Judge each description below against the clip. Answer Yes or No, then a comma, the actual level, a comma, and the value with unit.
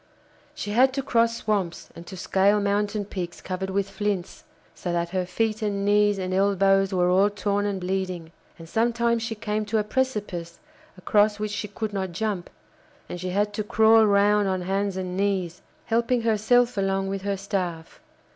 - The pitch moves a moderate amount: No, narrow, 2.2 semitones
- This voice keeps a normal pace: Yes, average, 180 wpm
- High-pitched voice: Yes, high, 200 Hz